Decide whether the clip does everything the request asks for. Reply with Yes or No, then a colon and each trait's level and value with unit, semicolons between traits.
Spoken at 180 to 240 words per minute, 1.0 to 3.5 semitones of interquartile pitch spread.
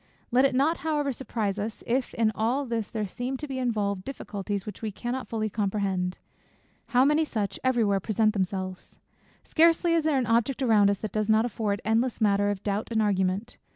No: average, 195 wpm; average, 4.2 semitones